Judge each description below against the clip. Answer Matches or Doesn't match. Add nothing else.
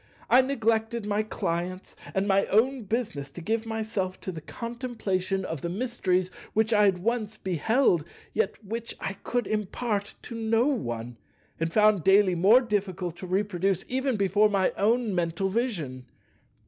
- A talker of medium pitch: Doesn't match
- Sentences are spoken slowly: Doesn't match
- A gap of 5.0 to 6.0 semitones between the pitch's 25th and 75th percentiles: Doesn't match